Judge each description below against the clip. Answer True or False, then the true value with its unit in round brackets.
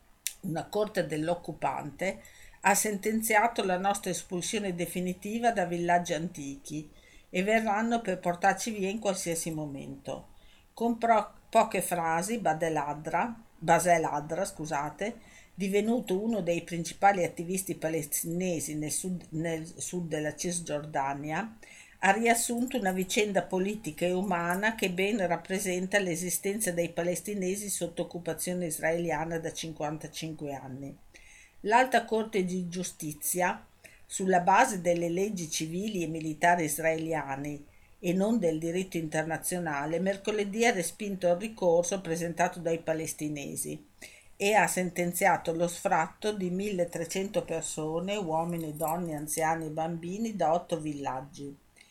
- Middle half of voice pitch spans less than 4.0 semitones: True (3.6 semitones)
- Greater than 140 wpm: False (115 wpm)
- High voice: False (175 Hz)